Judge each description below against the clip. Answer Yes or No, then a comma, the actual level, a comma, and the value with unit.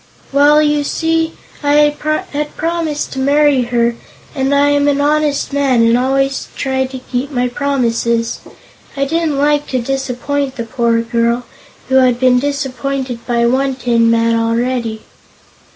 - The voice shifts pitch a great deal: No, average, 3.1 semitones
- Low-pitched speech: No, very high, 265 Hz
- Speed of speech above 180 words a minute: No, average, 150 wpm